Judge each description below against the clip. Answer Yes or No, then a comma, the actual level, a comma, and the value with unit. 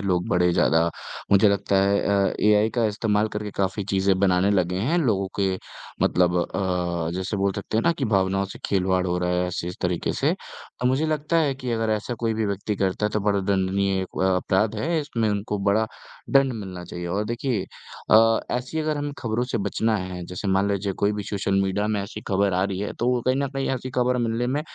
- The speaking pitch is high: No, low, 100 Hz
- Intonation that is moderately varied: Yes, average, 3.3 semitones